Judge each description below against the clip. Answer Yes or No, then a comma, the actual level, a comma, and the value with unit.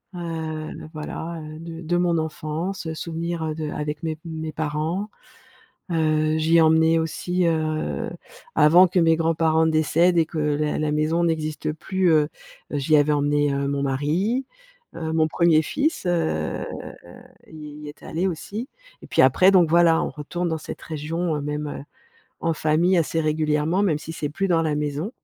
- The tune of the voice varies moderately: No, narrow, 1.8 semitones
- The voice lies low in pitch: No, medium, 160 Hz